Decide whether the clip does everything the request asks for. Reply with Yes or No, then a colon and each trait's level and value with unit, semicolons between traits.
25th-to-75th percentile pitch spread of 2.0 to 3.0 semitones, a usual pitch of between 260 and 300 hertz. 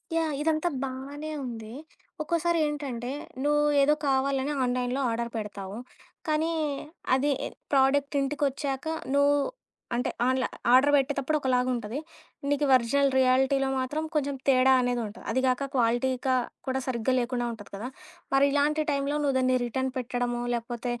Yes: narrow, 2.5 semitones; very high, 265 Hz